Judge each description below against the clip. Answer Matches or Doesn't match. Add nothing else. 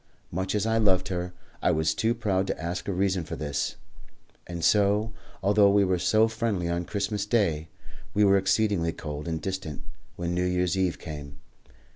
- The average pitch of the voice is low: Matches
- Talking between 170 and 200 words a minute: Matches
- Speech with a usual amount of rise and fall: Matches